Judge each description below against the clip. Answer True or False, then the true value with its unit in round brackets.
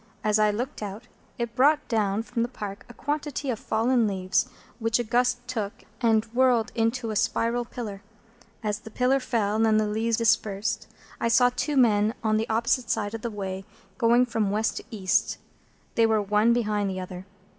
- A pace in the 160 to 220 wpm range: True (190 wpm)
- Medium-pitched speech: False (225 Hz)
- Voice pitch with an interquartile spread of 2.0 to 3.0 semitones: True (2.5 semitones)